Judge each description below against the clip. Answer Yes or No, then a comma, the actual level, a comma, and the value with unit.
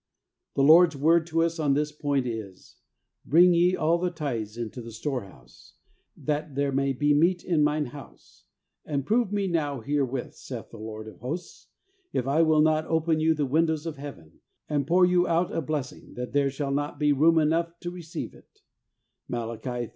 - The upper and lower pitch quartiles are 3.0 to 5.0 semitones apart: Yes, average, 3.4 semitones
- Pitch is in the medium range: Yes, medium, 150 Hz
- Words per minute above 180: Yes, average, 190 wpm